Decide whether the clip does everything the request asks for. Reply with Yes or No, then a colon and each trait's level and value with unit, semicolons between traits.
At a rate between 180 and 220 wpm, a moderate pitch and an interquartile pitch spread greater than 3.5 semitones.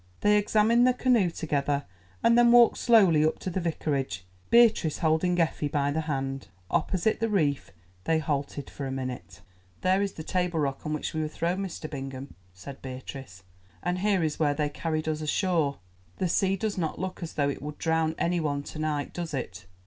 Yes: average, 195 wpm; medium, 160 Hz; average, 4.6 semitones